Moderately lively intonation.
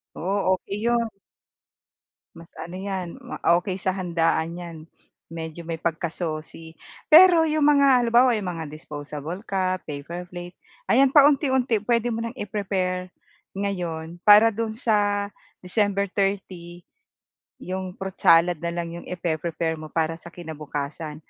Yes: average, 4.2 semitones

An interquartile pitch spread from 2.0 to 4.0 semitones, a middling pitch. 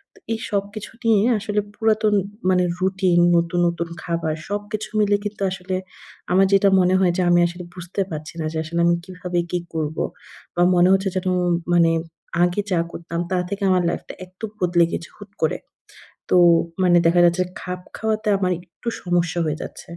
Yes: narrow, 2.5 semitones; medium, 180 Hz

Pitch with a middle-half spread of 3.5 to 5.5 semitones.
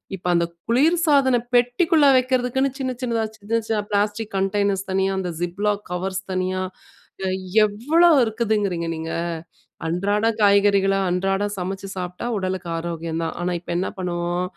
Yes: average, 4.1 semitones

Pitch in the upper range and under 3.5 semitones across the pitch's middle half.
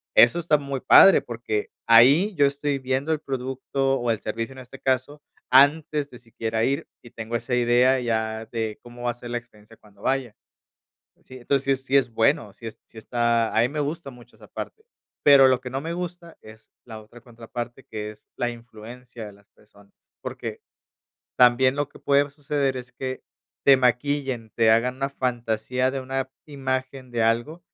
No: low, 125 Hz; average, 2.9 semitones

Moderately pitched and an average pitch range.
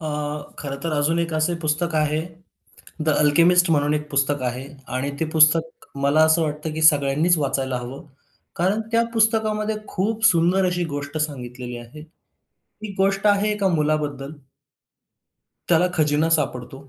Yes: medium, 155 Hz; average, 3.7 semitones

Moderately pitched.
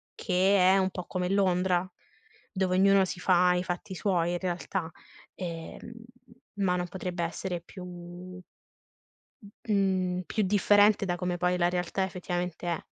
Yes: medium, 180 Hz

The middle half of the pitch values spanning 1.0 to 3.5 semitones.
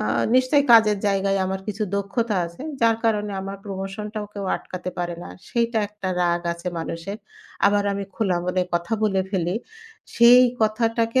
Yes: average, 2.9 semitones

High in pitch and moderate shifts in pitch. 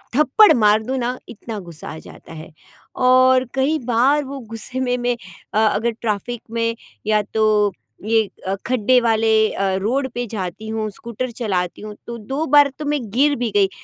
Yes: high, 235 Hz; average, 3.3 semitones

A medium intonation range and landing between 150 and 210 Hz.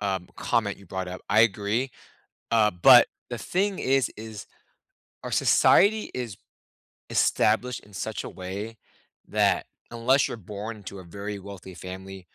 No: average, 3.4 semitones; low, 105 Hz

